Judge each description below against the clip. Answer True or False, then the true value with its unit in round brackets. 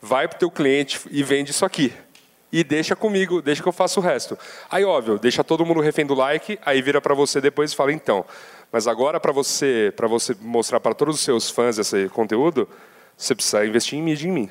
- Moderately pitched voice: True (145 Hz)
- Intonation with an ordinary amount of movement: True (4.3 semitones)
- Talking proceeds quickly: True (225 wpm)